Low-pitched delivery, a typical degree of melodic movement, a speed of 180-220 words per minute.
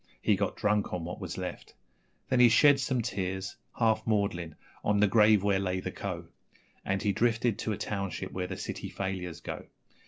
Yes: low, 100 Hz; average, 3.0 semitones; average, 190 wpm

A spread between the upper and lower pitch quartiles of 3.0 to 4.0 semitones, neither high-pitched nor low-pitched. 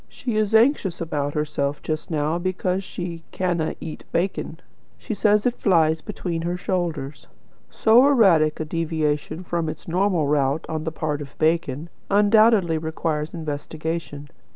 Yes: average, 3.3 semitones; medium, 165 Hz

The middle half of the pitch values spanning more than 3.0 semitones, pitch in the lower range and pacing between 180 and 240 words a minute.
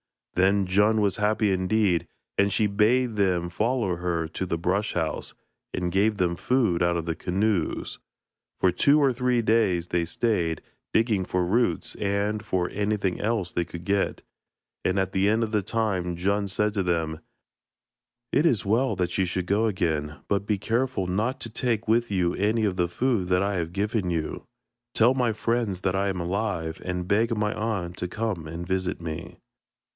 Yes: average, 3.8 semitones; low, 100 Hz; average, 185 wpm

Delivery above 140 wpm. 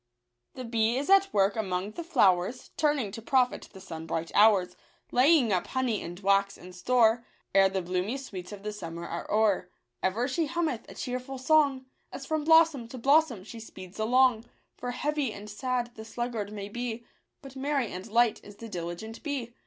Yes: average, 185 wpm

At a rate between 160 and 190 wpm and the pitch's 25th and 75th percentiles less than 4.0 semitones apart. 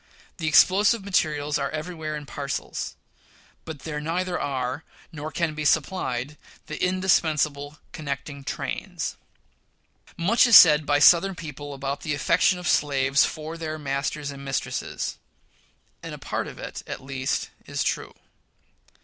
No: average, 140 wpm; average, 3.0 semitones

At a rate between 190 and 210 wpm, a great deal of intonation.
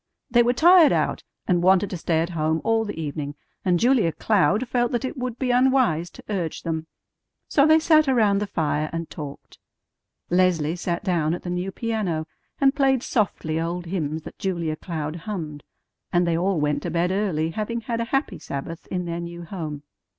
Yes: average, 195 wpm; wide, 6.1 semitones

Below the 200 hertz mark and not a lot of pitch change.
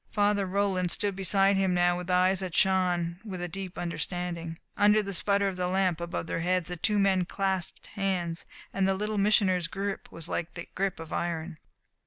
Yes: medium, 185 Hz; narrow, 2.0 semitones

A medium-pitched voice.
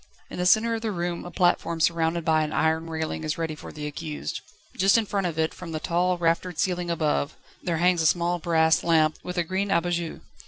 Yes: medium, 170 Hz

